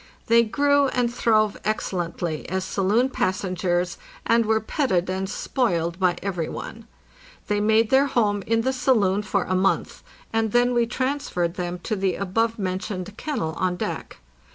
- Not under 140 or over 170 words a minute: Yes, average, 155 wpm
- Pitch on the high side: Yes, high, 205 Hz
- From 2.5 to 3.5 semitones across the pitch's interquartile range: No, average, 4.1 semitones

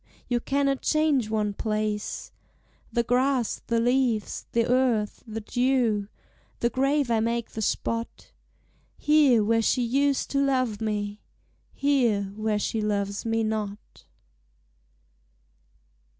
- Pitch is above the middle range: Yes, high, 230 Hz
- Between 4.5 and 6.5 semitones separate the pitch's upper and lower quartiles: No, average, 3.4 semitones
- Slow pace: Yes, slow, 120 wpm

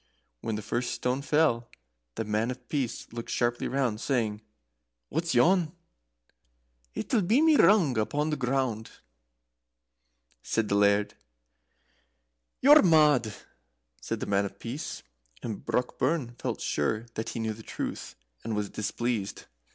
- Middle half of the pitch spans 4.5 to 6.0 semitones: Yes, average, 5.3 semitones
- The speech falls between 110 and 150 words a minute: Yes, average, 140 wpm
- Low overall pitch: Yes, low, 120 Hz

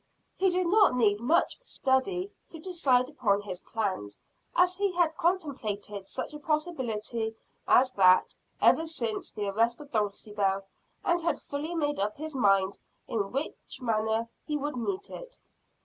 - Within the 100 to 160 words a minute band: Yes, average, 150 wpm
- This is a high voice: Yes, very high, 255 Hz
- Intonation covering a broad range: Yes, wide, 7.7 semitones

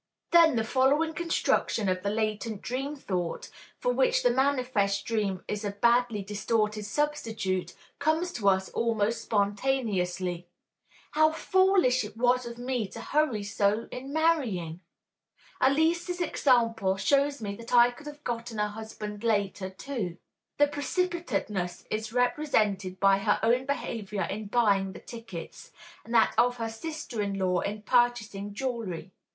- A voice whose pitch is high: Yes, high, 230 Hz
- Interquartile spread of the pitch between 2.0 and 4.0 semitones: No, average, 5.2 semitones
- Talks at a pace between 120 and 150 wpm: Yes, average, 145 wpm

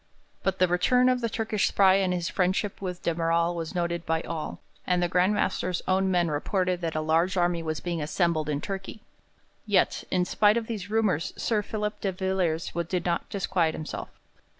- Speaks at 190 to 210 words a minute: Yes, average, 195 wpm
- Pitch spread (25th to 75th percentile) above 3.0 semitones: No, narrow, 2.6 semitones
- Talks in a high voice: No, medium, 180 Hz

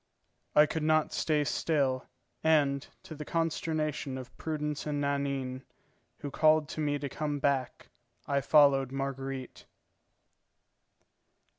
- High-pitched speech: No, medium, 145 Hz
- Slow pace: Yes, slow, 120 wpm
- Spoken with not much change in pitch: Yes, narrow, 2.1 semitones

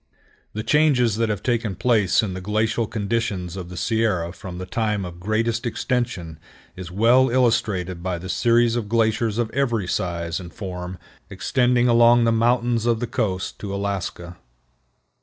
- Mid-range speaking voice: No, low, 110 Hz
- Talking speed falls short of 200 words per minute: Yes, average, 160 wpm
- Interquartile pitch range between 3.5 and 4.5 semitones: Yes, average, 4.2 semitones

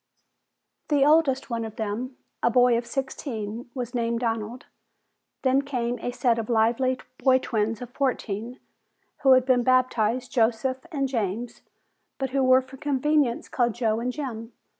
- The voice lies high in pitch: Yes, high, 245 Hz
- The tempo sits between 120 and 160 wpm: Yes, average, 155 wpm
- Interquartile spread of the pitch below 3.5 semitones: Yes, narrow, 2.4 semitones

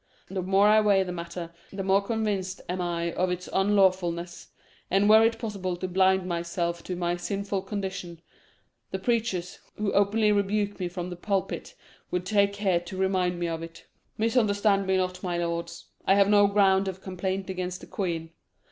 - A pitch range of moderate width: No, narrow, 2.2 semitones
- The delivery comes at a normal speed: Yes, average, 180 wpm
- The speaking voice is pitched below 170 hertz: No, high, 190 Hz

